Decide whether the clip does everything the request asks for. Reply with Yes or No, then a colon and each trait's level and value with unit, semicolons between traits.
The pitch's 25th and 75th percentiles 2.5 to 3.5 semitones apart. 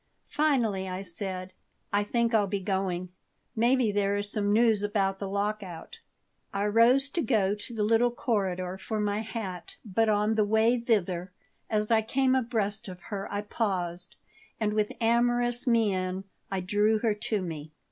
Yes: average, 2.8 semitones